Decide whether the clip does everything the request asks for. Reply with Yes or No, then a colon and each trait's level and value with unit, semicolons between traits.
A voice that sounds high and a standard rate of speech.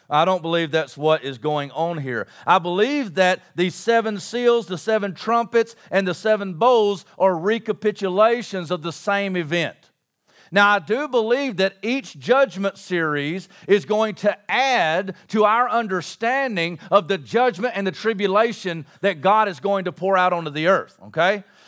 Yes: high, 195 Hz; average, 165 wpm